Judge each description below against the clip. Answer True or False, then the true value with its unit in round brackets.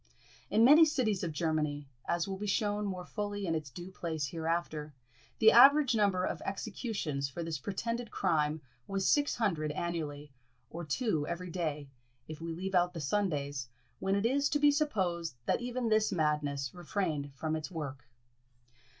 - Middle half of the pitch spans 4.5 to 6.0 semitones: True (5.4 semitones)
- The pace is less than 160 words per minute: False (165 wpm)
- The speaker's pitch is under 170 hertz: False (175 Hz)